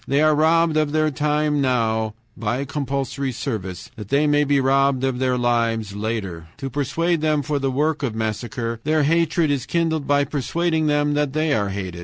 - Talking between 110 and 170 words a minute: No, average, 190 wpm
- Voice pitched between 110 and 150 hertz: Yes, medium, 140 Hz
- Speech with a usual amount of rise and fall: Yes, average, 4.5 semitones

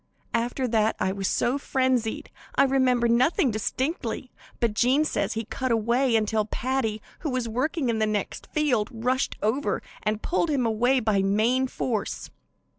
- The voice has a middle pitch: No, high, 240 Hz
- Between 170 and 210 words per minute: No, average, 160 wpm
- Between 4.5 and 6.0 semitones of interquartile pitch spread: No, average, 3.1 semitones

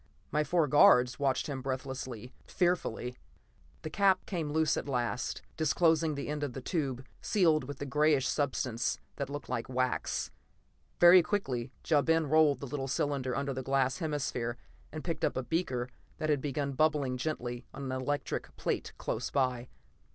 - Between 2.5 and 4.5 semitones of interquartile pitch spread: Yes, average, 3.3 semitones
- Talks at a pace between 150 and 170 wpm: Yes, average, 165 wpm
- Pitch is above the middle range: No, medium, 140 Hz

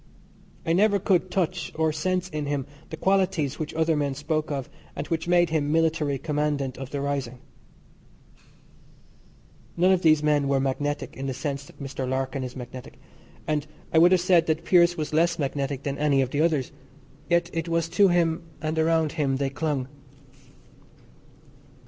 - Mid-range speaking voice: Yes, medium, 155 Hz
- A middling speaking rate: Yes, average, 175 wpm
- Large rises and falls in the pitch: No, average, 3.2 semitones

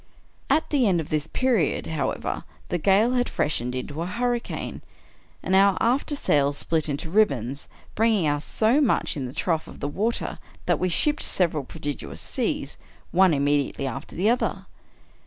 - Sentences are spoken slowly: No, average, 170 wpm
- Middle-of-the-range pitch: Yes, medium, 175 Hz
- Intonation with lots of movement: Yes, wide, 7.7 semitones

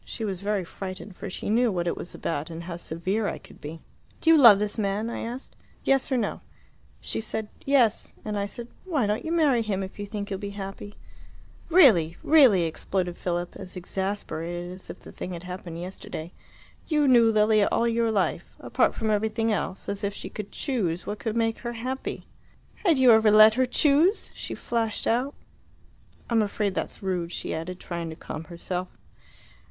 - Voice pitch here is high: Yes, high, 205 Hz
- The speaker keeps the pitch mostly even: No, average, 4.2 semitones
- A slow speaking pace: No, average, 195 wpm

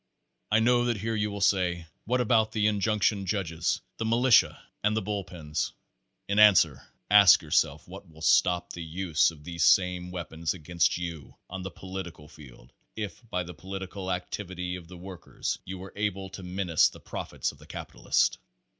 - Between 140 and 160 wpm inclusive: No, average, 185 wpm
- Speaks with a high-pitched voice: No, very low, 95 Hz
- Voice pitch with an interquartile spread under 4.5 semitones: Yes, average, 3.3 semitones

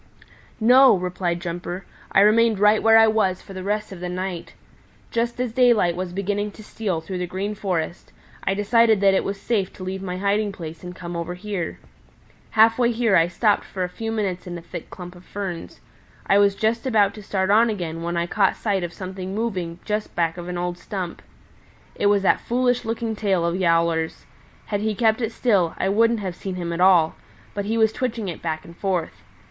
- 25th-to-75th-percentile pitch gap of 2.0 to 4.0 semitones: Yes, average, 3.5 semitones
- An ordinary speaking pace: No, fast, 215 wpm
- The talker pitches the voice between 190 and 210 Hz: Yes, high, 195 Hz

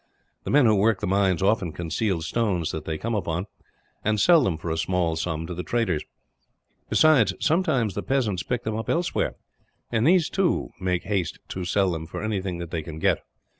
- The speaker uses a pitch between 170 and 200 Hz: No, very low, 95 Hz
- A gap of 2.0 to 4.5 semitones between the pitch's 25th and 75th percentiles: No, average, 5.0 semitones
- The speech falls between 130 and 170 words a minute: No, average, 200 wpm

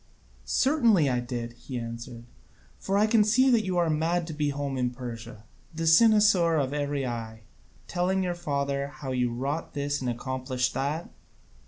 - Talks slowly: No, average, 170 wpm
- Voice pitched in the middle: Yes, medium, 145 Hz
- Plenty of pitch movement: Yes, wide, 5.8 semitones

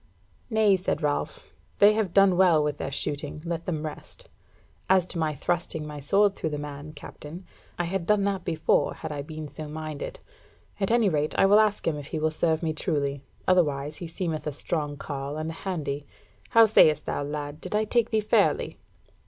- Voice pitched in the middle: Yes, medium, 160 Hz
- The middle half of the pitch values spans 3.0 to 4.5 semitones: Yes, average, 4.2 semitones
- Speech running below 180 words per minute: No, average, 200 wpm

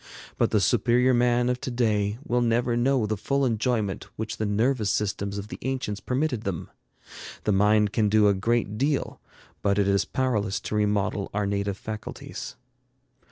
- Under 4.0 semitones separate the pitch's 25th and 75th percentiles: Yes, average, 3.2 semitones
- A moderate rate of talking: Yes, average, 170 wpm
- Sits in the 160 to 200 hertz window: No, low, 110 Hz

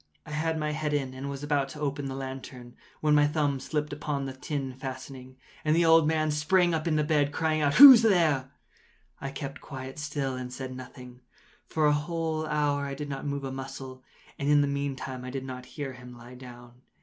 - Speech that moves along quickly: Yes, fast, 210 wpm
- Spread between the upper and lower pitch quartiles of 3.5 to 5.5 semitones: No, narrow, 2.4 semitones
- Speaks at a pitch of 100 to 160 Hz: Yes, medium, 140 Hz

